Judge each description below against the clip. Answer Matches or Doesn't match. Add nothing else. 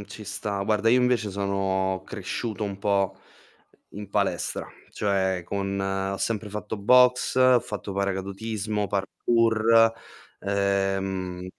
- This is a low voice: Matches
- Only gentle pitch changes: Matches